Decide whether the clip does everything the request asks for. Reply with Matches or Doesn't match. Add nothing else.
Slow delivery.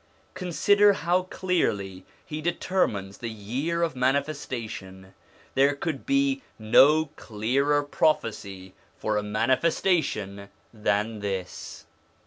Matches